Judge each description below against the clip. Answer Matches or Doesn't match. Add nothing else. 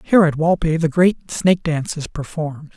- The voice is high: Doesn't match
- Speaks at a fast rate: Doesn't match